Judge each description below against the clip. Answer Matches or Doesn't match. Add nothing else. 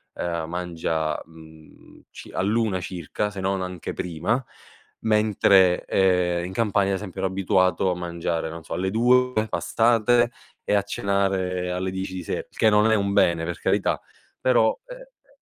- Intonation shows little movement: Doesn't match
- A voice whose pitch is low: Matches